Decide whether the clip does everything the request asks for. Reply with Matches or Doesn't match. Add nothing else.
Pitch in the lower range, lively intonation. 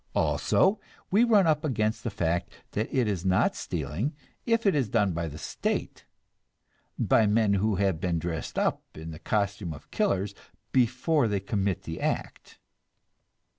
Matches